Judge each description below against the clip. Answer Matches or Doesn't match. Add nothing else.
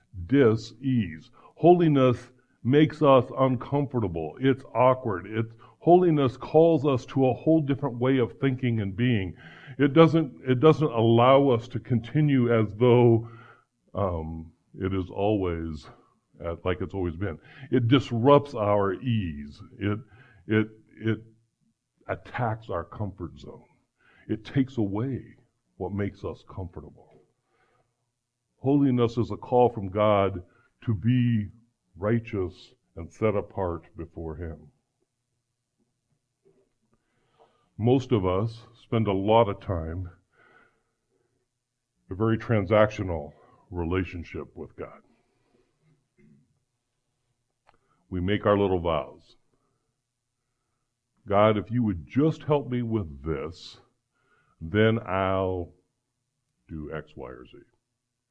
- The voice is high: Doesn't match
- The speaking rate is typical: Doesn't match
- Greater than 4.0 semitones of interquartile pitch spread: Matches